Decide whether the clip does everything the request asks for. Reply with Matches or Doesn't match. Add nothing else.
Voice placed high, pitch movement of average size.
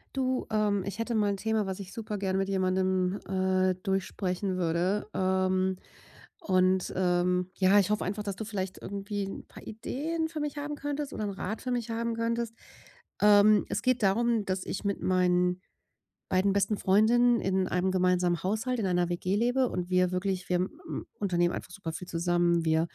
Matches